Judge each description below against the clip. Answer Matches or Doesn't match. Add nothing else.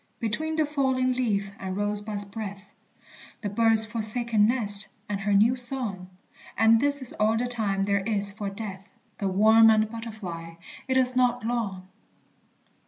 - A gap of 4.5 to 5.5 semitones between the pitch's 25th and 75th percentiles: Doesn't match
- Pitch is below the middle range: Doesn't match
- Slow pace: Doesn't match